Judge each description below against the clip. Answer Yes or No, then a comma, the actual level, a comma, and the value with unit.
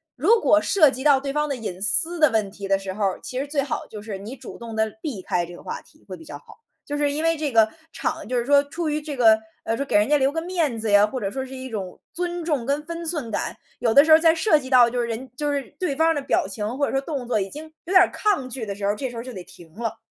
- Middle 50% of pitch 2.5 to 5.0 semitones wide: No, wide, 5.6 semitones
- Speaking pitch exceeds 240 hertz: Yes, very high, 265 Hz